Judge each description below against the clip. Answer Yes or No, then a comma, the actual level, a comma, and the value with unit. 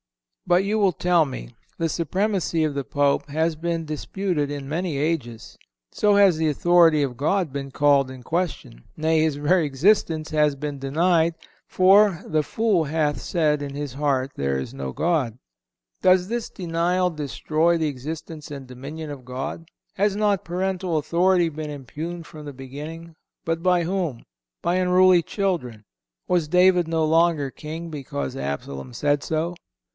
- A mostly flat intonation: No, average, 3.8 semitones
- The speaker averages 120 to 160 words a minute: Yes, average, 155 wpm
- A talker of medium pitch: Yes, medium, 160 Hz